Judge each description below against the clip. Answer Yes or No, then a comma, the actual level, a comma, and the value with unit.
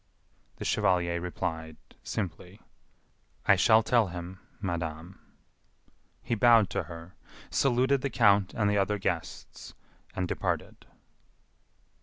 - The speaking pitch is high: No, very low, 95 Hz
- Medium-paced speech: No, slow, 110 wpm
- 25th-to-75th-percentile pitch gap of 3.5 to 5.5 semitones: Yes, average, 4.4 semitones